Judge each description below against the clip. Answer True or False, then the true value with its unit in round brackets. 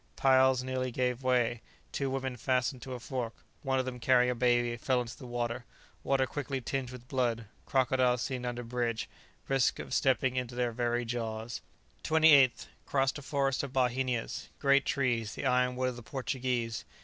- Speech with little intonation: True (1.6 semitones)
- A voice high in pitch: False (125 Hz)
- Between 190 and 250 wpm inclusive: False (175 wpm)